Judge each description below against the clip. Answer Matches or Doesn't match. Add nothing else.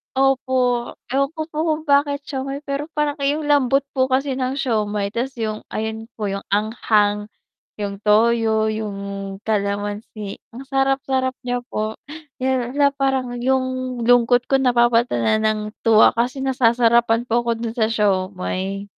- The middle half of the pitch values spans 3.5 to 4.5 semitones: Matches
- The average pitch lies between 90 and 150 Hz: Doesn't match